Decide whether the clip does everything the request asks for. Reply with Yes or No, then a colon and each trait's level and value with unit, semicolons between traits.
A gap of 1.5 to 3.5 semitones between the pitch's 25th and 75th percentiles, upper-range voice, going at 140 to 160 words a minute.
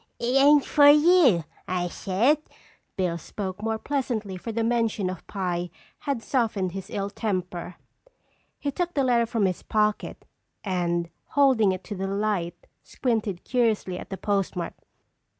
No: average, 4.7 semitones; high, 210 Hz; average, 150 wpm